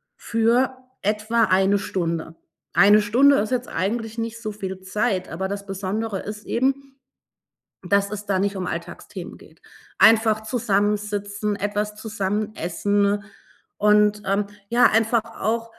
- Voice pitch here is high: Yes, high, 210 Hz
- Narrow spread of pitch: Yes, narrow, 2.1 semitones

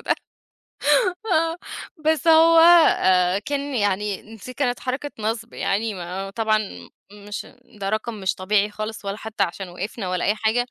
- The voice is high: Yes, high, 215 Hz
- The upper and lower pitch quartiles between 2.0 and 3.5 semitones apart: No, average, 3.9 semitones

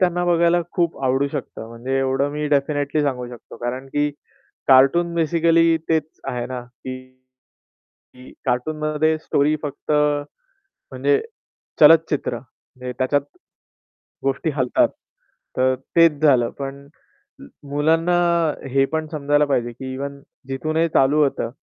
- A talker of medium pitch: Yes, medium, 145 Hz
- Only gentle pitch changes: No, average, 3.2 semitones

